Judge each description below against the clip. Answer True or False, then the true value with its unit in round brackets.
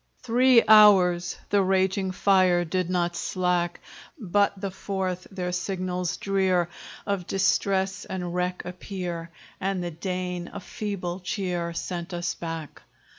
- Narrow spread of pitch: True (1.6 semitones)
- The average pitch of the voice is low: False (185 Hz)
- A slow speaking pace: True (125 wpm)